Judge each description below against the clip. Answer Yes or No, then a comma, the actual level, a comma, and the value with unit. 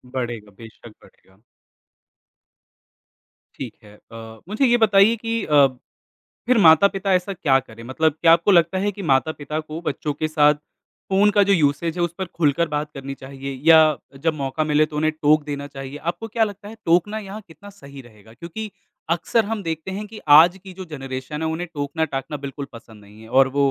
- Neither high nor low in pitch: Yes, medium, 155 Hz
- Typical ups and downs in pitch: No, wide, 5.7 semitones